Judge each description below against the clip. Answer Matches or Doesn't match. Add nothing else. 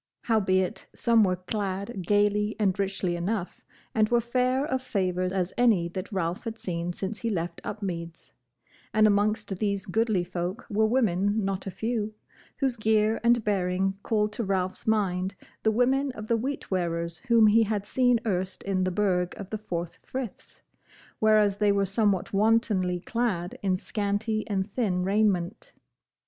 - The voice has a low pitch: Doesn't match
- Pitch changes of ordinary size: Matches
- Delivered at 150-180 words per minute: Matches